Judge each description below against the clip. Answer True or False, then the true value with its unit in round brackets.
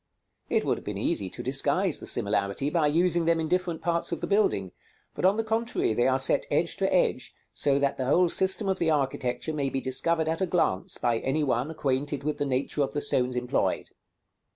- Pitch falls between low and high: True (145 Hz)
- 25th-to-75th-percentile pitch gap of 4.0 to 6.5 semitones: True (4.5 semitones)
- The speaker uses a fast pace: True (220 wpm)